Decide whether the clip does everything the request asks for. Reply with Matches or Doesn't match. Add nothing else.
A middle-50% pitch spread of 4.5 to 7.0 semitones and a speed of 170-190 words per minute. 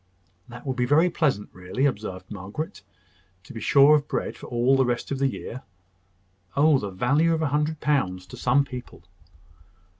Matches